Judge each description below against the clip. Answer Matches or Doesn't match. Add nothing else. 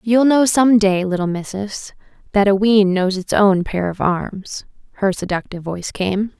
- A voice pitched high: Matches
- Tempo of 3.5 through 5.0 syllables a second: Matches